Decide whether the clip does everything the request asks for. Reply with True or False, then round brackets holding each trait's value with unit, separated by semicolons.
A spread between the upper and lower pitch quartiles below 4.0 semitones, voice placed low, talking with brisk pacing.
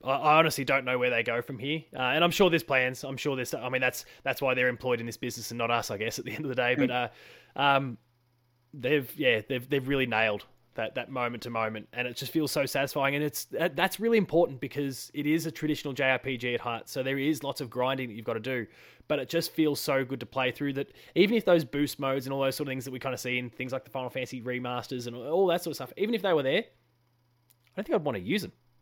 True (2.8 semitones; 130 Hz; 280 wpm)